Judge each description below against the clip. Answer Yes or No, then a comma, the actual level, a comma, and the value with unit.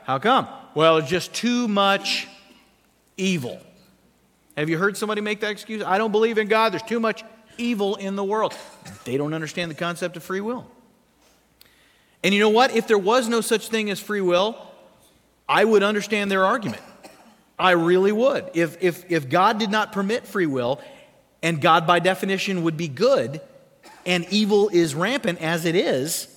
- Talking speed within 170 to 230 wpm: Yes, average, 180 wpm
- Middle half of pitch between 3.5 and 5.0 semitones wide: Yes, average, 3.8 semitones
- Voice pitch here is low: No, high, 200 Hz